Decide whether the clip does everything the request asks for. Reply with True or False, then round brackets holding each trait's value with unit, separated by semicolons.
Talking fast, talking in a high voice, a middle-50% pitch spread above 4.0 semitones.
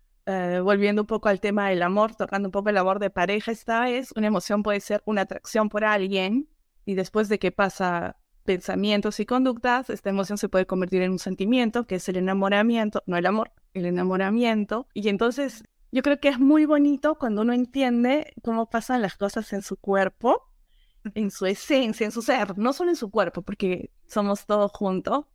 False (195 wpm; 210 Hz; 3.4 semitones)